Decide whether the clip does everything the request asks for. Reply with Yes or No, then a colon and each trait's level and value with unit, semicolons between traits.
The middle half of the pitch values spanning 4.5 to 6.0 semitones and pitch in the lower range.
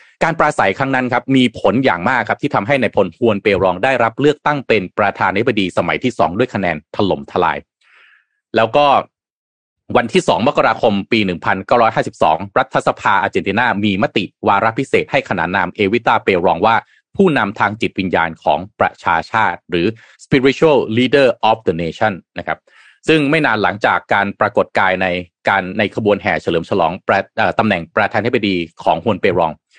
Yes: average, 5.2 semitones; low, 105 Hz